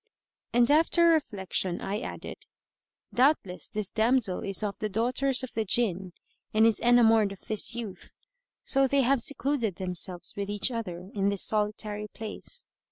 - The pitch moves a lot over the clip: No, average, 3.7 semitones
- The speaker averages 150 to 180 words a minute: Yes, average, 155 wpm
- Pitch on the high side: Yes, high, 220 Hz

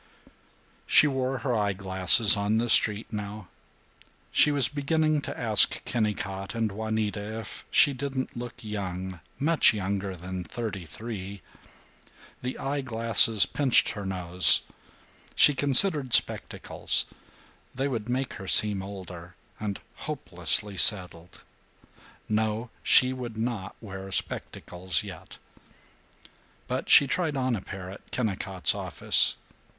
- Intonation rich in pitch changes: No, average, 4.7 semitones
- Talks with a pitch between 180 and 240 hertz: No, low, 110 Hz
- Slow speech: Yes, slow, 125 wpm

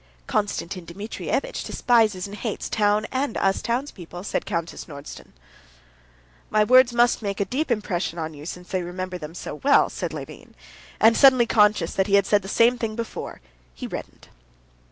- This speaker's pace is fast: No, average, 175 wpm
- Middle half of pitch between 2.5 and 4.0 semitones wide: No, average, 4.7 semitones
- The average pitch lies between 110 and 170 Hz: No, high, 205 Hz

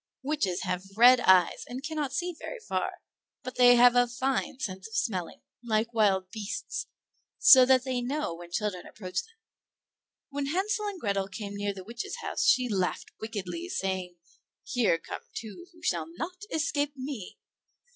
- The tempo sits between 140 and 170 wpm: Yes, average, 165 wpm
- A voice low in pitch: No, high, 235 Hz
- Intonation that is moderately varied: No, wide, 6.2 semitones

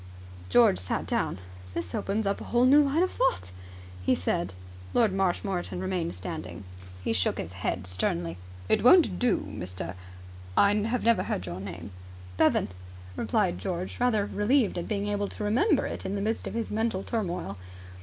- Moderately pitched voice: No, high, 195 Hz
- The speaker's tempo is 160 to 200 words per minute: Yes, average, 165 wpm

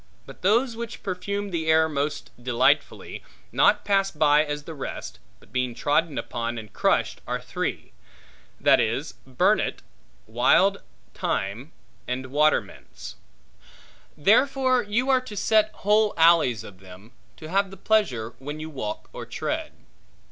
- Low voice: No, medium, 155 Hz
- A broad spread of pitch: Yes, wide, 8.1 semitones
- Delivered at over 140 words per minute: No, slow, 135 wpm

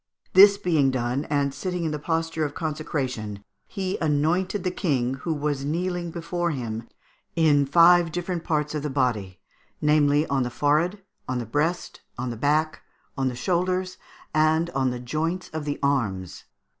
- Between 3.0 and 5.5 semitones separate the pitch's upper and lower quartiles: Yes, average, 4.2 semitones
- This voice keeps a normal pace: Yes, average, 165 wpm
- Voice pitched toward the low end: No, medium, 150 Hz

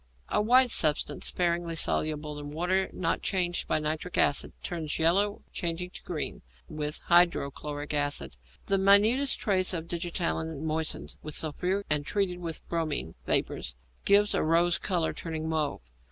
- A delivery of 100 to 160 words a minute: Yes, average, 155 wpm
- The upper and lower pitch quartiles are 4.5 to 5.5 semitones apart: No, average, 3.1 semitones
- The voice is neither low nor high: Yes, medium, 165 Hz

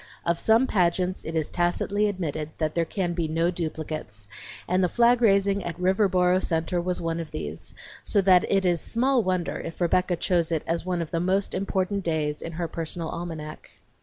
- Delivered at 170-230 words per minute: Yes, average, 190 wpm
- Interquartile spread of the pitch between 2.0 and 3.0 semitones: Yes, narrow, 2.5 semitones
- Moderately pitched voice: Yes, medium, 175 Hz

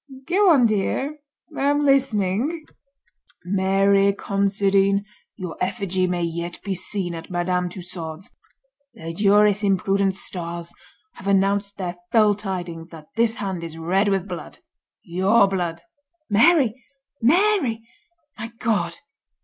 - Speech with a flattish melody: No, average, 3.4 semitones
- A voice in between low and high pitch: No, high, 195 Hz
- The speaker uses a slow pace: Yes, slow, 115 wpm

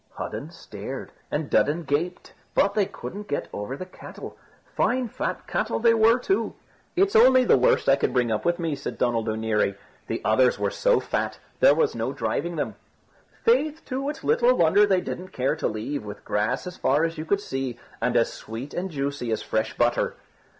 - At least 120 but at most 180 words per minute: No, average, 195 wpm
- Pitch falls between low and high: Yes, medium, 160 Hz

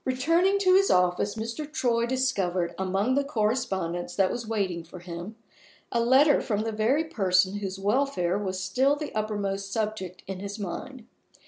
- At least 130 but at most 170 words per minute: Yes, average, 160 wpm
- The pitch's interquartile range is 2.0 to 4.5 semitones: No, wide, 5.5 semitones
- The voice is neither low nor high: No, high, 215 Hz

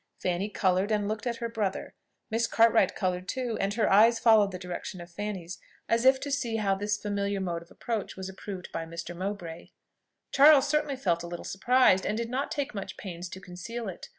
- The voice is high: Yes, high, 205 Hz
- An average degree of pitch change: Yes, average, 4.1 semitones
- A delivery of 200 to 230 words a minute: Yes, fast, 205 wpm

